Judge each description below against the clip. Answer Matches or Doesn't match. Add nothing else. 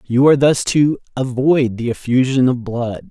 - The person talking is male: Matches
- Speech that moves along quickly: Doesn't match